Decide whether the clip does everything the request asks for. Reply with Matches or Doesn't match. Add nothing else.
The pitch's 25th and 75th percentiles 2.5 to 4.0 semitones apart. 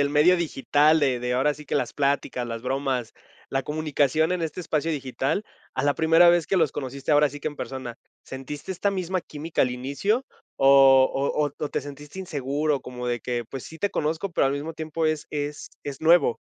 Matches